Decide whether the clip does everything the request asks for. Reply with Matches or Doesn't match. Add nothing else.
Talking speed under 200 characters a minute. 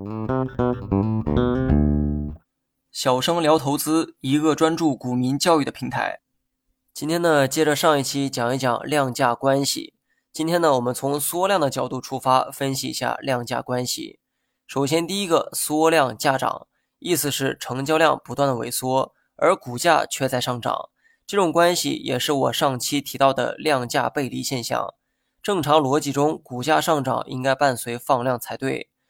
Doesn't match